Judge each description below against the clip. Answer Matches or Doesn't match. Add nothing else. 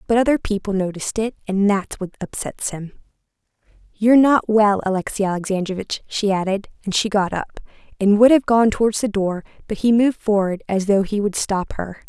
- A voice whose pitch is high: Matches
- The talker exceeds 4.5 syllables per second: Matches